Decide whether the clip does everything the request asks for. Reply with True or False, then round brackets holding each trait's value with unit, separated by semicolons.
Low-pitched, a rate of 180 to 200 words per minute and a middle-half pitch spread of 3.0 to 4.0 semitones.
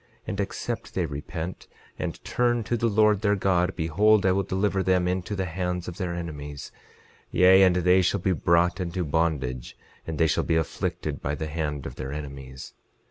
True (90 Hz; 190 wpm; 3.3 semitones)